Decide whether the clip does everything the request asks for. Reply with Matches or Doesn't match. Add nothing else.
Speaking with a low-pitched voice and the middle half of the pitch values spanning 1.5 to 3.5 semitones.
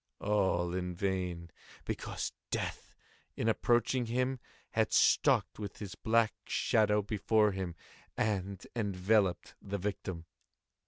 Matches